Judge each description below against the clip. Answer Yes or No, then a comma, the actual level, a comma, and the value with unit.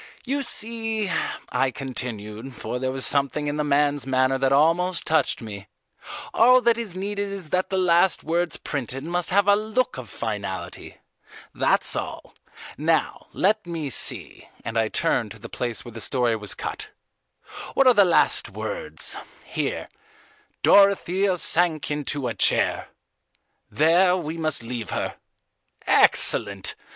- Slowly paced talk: No, average, 145 wpm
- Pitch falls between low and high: Yes, medium, 155 Hz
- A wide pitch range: Yes, wide, 6.9 semitones